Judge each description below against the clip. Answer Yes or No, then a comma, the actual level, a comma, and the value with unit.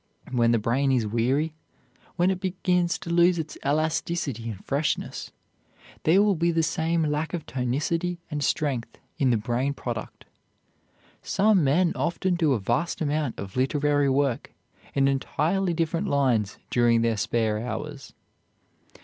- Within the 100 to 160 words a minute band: Yes, average, 145 wpm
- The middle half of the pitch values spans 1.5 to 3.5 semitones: No, wide, 5.6 semitones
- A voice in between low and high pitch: Yes, medium, 145 Hz